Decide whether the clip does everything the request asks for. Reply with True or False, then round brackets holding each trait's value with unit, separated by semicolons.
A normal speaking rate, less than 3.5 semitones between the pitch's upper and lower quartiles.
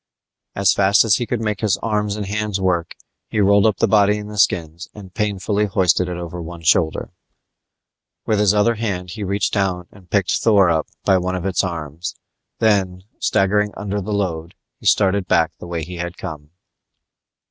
True (190 wpm; 2.8 semitones)